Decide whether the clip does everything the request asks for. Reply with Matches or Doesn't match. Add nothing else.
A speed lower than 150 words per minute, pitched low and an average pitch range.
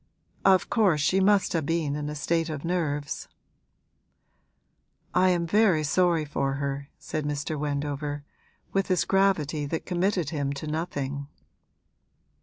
Doesn't match